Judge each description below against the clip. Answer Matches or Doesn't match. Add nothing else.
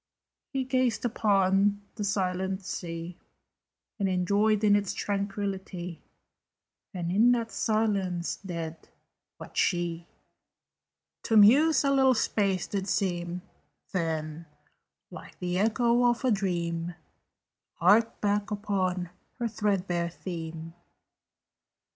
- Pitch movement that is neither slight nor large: Matches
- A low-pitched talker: Doesn't match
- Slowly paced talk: Matches